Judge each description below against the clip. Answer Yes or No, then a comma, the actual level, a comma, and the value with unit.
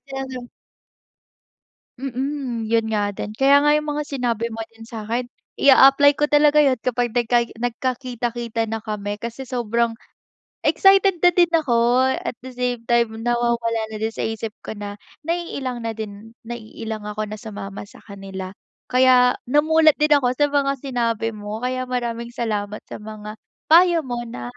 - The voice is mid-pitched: No, high, 240 Hz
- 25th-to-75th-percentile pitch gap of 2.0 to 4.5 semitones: Yes, average, 3.3 semitones